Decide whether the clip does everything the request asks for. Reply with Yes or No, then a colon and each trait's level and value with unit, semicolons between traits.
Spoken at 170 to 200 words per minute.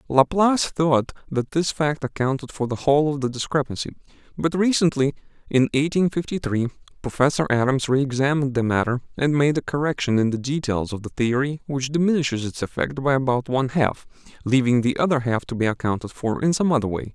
Yes: average, 190 wpm